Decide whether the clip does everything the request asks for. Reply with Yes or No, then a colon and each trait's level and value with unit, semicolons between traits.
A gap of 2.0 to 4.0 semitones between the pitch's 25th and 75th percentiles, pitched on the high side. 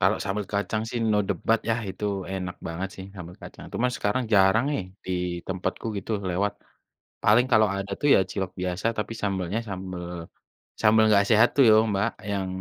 No: narrow, 2.6 semitones; low, 100 Hz